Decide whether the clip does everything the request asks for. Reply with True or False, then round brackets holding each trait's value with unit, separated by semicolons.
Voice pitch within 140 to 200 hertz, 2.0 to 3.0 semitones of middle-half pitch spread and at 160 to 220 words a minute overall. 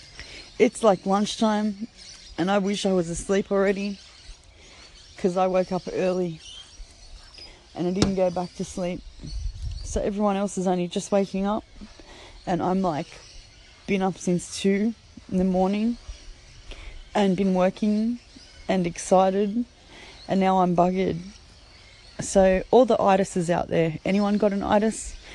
False (190 Hz; 2.5 semitones; 140 wpm)